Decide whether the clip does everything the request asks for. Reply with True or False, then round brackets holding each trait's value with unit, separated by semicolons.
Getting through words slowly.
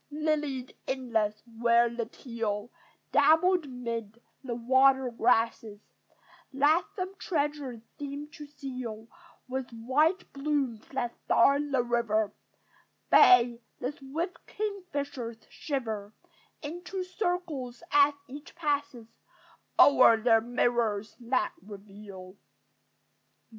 True (95 wpm)